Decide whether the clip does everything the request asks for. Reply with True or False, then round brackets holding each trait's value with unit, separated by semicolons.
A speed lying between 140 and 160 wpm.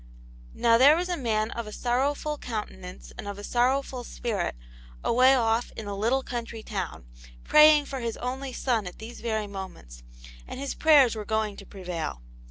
False (180 wpm)